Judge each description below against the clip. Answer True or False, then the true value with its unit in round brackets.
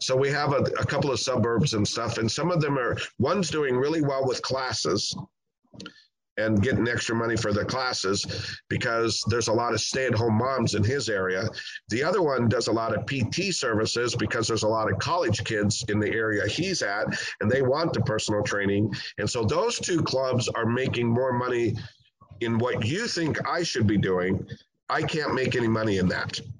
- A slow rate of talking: False (200 wpm)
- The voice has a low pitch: True (115 Hz)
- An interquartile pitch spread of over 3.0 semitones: True (3.5 semitones)